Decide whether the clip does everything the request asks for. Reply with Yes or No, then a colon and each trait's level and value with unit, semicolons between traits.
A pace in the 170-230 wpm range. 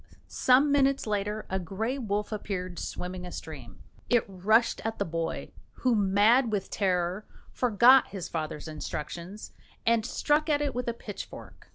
No: average, 155 wpm